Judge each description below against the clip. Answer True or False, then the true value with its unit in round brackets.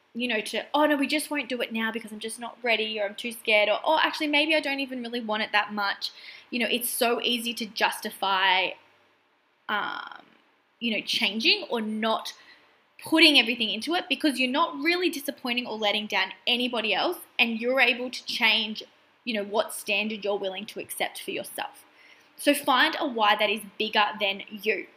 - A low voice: False (235 Hz)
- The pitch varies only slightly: False (4.6 semitones)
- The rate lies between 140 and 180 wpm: False (200 wpm)